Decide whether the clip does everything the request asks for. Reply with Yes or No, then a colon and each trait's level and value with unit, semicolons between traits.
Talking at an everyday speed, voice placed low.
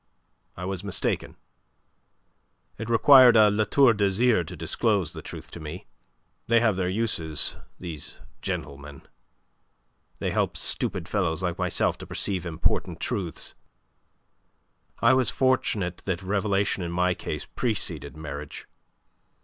No: slow, 125 wpm; very low, 95 Hz